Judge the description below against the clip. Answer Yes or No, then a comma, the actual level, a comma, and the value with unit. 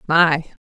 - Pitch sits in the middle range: Yes, medium, 160 Hz